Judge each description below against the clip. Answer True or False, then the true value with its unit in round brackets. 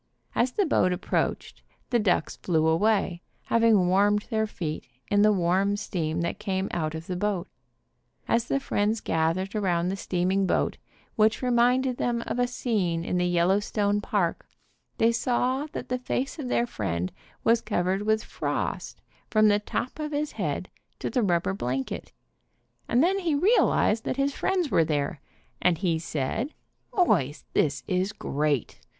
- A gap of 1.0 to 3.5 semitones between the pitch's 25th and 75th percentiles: False (5.5 semitones)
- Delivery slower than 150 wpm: False (165 wpm)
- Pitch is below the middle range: False (205 Hz)